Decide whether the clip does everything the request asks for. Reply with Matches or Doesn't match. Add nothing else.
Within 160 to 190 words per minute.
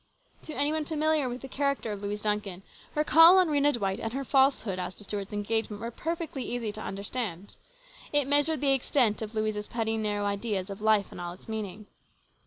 Doesn't match